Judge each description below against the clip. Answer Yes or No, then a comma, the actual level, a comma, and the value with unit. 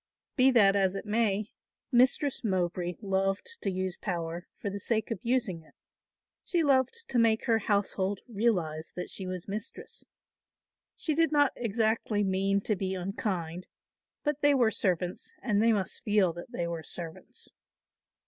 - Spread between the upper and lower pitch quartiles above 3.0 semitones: Yes, average, 4.1 semitones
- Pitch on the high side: Yes, high, 200 Hz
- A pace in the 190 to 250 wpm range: No, average, 160 wpm